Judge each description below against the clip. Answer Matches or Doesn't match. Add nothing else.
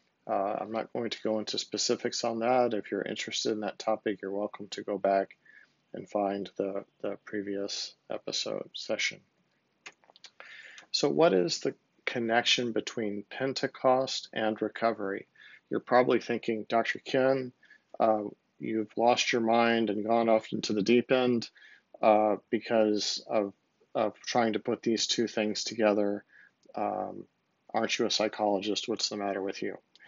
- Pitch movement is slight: Matches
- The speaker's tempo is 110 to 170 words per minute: Matches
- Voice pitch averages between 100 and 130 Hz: Matches